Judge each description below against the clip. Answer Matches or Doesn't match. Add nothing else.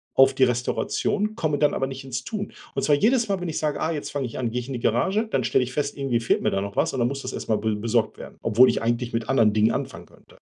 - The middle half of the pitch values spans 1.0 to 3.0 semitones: Doesn't match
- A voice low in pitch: Matches